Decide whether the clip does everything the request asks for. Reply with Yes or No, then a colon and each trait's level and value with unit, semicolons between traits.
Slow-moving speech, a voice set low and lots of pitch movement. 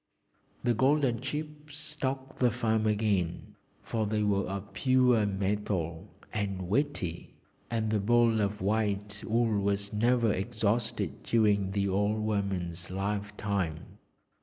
No: slow, 125 wpm; low, 105 Hz; average, 3.0 semitones